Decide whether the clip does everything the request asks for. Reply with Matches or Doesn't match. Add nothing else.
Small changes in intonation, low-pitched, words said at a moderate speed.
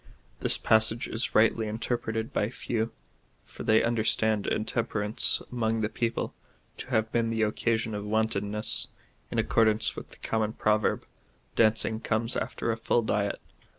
Matches